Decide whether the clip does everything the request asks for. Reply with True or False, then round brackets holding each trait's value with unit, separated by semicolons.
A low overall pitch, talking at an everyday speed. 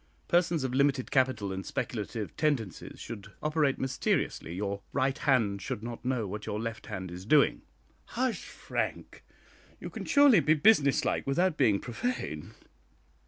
True (130 Hz; 150 wpm)